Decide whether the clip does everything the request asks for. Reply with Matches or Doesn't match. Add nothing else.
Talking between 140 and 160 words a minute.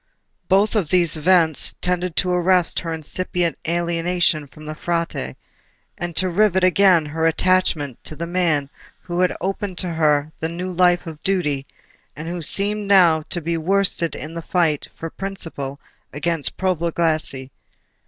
Matches